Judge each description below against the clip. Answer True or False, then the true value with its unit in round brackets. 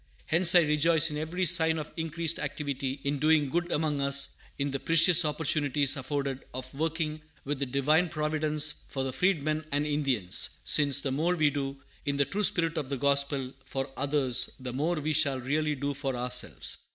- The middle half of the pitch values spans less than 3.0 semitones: True (2.4 semitones)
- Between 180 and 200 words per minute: True (185 wpm)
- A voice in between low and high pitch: True (145 Hz)